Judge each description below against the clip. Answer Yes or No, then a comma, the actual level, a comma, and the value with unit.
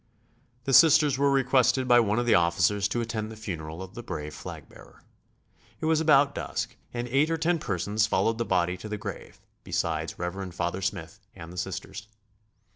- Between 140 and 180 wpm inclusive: No, average, 190 wpm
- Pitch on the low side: Yes, low, 110 Hz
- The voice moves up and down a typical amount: No, wide, 6.3 semitones